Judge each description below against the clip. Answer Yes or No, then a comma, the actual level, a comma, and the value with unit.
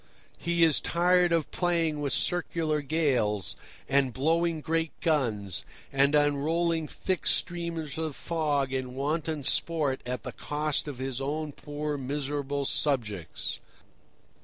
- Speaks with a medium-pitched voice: Yes, medium, 150 Hz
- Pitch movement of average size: Yes, average, 3.2 semitones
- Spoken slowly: Yes, slow, 125 wpm